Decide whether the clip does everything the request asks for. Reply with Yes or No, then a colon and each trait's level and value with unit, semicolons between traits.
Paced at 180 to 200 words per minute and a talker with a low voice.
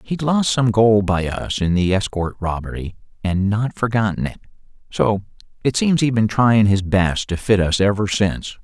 Yes: average, 190 wpm; low, 105 Hz